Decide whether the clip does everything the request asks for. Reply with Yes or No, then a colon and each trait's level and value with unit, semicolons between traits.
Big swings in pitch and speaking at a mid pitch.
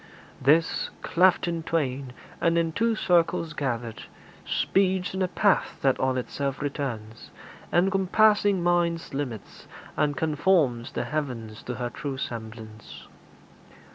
Yes: wide, 5.9 semitones; medium, 150 Hz